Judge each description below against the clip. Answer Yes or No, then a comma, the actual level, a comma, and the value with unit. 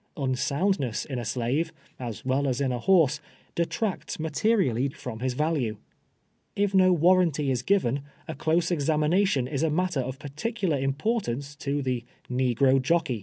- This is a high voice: No, medium, 145 Hz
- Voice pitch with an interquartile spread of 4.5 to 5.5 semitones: Yes, average, 4.9 semitones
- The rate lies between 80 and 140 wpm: No, average, 165 wpm